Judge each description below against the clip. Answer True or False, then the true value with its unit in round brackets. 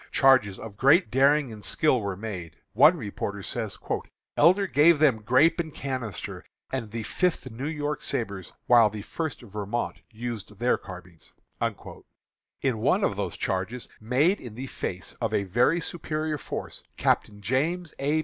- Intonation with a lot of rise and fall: True (6.1 semitones)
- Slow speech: False (155 wpm)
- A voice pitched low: True (120 Hz)